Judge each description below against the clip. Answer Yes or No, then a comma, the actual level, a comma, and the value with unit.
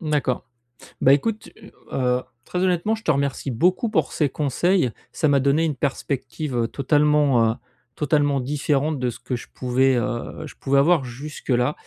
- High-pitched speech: No, medium, 140 Hz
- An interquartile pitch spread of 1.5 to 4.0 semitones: Yes, average, 3.3 semitones